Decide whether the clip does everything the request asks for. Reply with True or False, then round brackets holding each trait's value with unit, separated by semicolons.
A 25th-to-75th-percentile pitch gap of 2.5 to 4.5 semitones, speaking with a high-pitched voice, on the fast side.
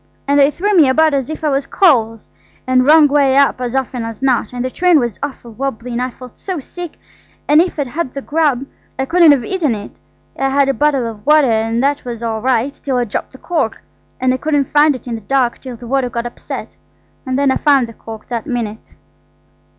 True (3.5 semitones; 265 Hz; 230 wpm)